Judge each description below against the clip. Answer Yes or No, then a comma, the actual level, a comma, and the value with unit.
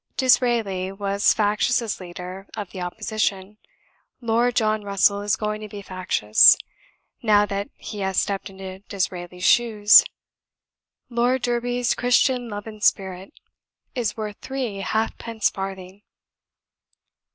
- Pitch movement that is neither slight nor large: Yes, average, 3.1 semitones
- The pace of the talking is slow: Yes, slow, 125 wpm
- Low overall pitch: No, high, 205 Hz